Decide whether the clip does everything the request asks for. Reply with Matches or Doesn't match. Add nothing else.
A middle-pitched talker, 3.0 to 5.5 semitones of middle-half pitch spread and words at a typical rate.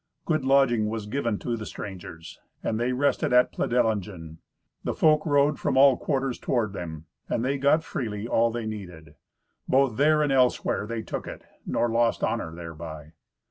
Doesn't match